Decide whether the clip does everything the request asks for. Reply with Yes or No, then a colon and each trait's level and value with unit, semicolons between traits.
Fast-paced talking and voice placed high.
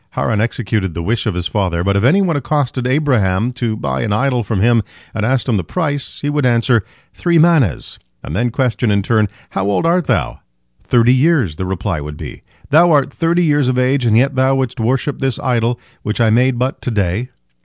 No: fast, 215 wpm; low, 120 Hz